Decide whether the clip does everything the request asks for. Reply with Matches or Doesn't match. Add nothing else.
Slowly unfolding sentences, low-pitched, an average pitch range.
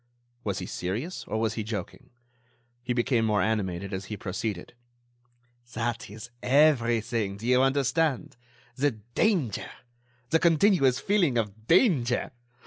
Matches